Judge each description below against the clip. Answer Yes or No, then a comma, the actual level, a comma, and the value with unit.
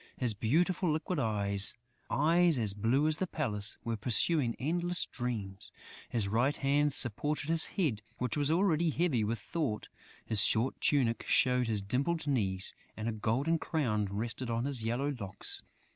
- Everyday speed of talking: Yes, average, 160 wpm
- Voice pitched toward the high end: No, low, 125 Hz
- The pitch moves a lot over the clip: Yes, wide, 5.8 semitones